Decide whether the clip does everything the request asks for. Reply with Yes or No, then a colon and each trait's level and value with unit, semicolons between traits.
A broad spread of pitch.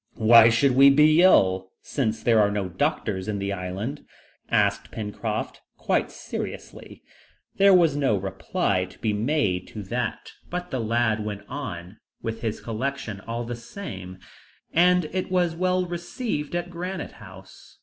Yes: wide, 7.6 semitones